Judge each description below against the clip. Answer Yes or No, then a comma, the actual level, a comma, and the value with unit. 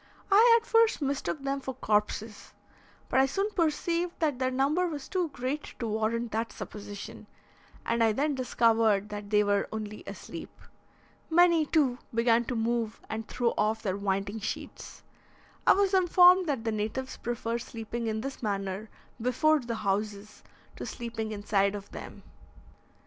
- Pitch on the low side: No, high, 235 Hz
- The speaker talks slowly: No, average, 155 wpm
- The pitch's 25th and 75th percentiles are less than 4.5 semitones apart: No, average, 5.2 semitones